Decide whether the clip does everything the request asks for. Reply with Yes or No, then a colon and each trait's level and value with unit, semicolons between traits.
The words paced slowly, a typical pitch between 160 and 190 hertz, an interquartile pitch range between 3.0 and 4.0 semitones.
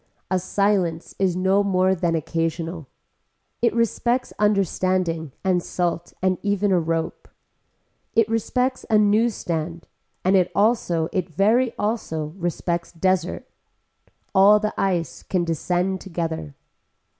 Yes: slow, 120 wpm; medium, 185 Hz; average, 3.5 semitones